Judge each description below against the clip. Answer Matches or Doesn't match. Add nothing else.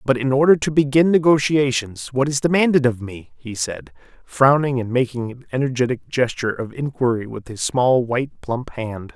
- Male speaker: Matches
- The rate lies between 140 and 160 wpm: Doesn't match